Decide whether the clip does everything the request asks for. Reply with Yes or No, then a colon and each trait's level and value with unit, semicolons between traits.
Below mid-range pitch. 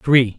Yes: low, 125 Hz